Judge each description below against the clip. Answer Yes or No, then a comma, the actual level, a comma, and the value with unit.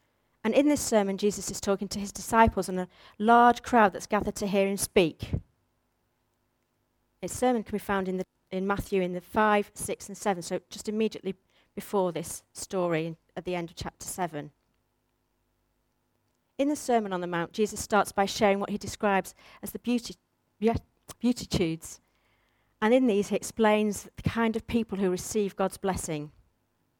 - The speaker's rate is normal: Yes, average, 170 wpm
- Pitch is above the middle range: Yes, high, 195 Hz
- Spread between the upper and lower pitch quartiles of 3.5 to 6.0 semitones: Yes, average, 4.2 semitones